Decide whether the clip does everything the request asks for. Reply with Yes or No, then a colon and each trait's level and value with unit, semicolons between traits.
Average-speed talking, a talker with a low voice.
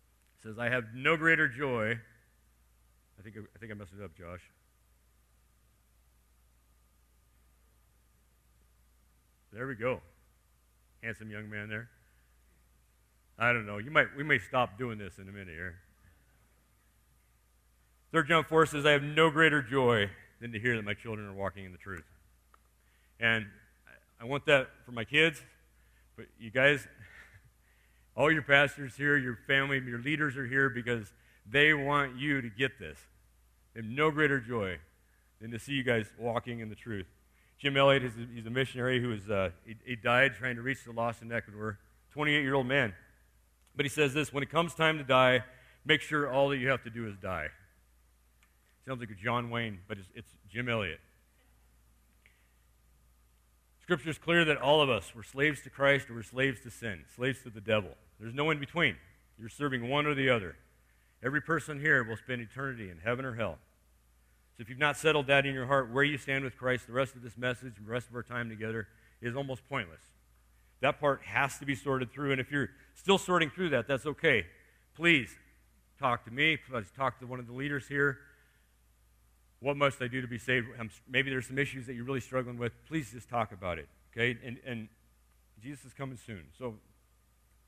Yes: average, 190 wpm; low, 115 Hz